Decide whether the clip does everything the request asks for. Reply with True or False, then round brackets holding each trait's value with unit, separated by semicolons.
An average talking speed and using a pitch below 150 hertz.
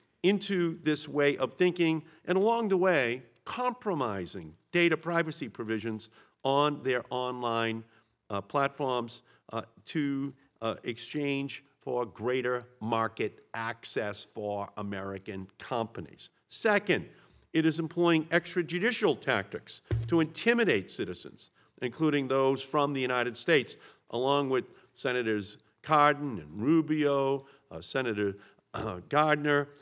False (110 wpm; 135 Hz)